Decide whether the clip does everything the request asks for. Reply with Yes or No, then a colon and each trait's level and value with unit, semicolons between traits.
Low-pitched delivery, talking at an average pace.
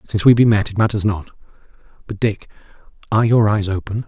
Yes: low, 105 Hz; average, 190 wpm